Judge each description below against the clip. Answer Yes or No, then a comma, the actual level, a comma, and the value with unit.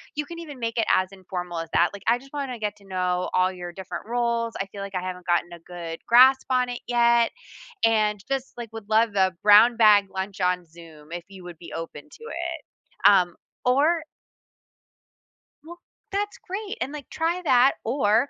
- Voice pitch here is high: Yes, high, 215 Hz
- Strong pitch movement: Yes, wide, 5.9 semitones